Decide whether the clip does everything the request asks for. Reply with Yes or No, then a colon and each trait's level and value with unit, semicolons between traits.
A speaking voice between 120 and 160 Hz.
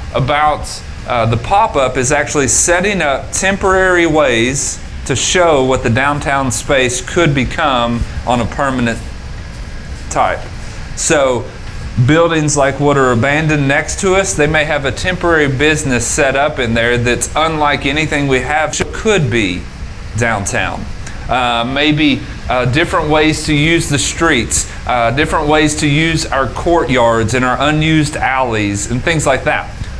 Yes: low, 135 Hz